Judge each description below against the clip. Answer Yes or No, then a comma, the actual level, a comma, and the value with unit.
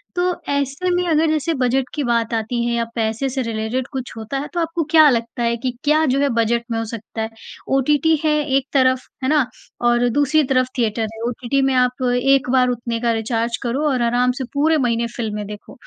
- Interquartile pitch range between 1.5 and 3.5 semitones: Yes, average, 3.2 semitones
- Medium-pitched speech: No, very high, 250 Hz